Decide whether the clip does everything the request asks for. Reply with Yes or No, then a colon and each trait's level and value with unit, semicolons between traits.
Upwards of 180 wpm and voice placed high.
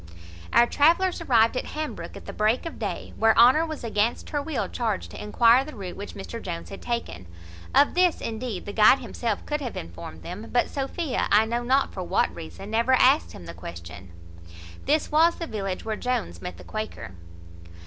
Yes: average, 200 wpm; high, 225 Hz